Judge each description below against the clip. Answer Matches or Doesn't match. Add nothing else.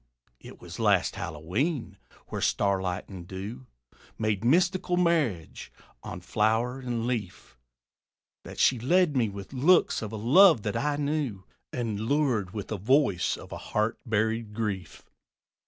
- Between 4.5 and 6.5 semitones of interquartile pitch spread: Matches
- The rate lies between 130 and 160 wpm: Matches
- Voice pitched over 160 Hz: Doesn't match